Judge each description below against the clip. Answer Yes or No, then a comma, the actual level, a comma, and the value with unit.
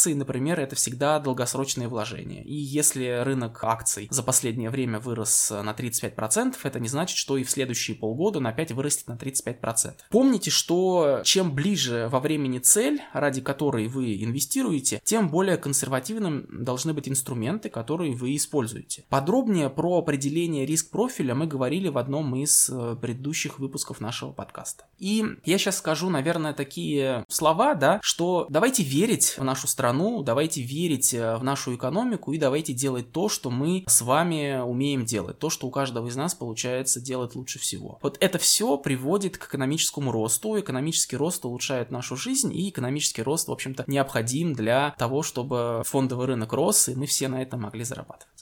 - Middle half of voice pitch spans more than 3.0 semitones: Yes, average, 4.1 semitones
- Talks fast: Yes, fast, 165 wpm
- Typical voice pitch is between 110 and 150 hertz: Yes, low, 135 Hz